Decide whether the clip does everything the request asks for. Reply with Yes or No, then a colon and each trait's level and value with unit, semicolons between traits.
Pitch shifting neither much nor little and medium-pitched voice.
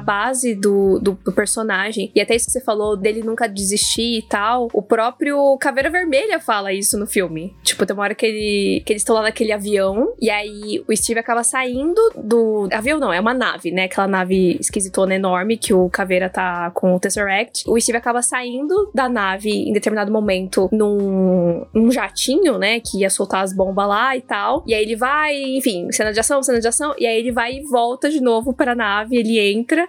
No: average, 3.9 semitones; high, 220 Hz